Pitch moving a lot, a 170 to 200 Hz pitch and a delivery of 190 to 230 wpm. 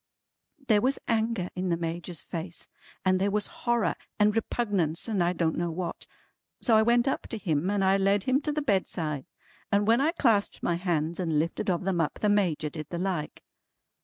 No: average, 4.3 semitones; high, 190 Hz; average, 200 wpm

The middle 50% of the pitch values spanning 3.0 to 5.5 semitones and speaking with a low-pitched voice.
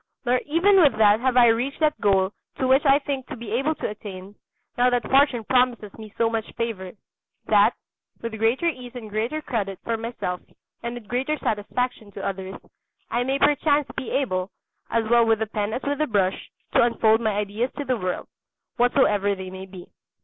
No: average, 4.0 semitones; high, 230 Hz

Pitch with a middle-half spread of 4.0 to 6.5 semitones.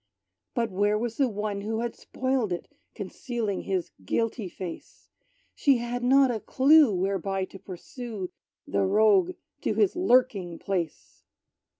Yes: average, 4.3 semitones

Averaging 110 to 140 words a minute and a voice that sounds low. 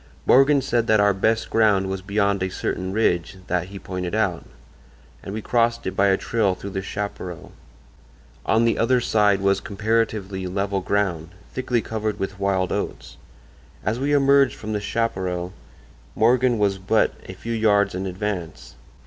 No: average, 165 wpm; low, 100 Hz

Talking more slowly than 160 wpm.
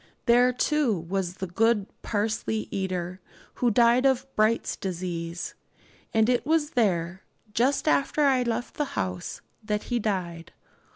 Yes: slow, 135 wpm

